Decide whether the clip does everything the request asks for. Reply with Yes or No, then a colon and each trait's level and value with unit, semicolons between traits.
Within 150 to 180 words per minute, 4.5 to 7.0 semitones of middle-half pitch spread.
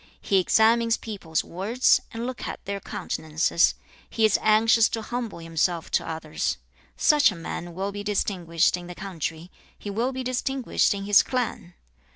Yes: average, 165 wpm; average, 4.9 semitones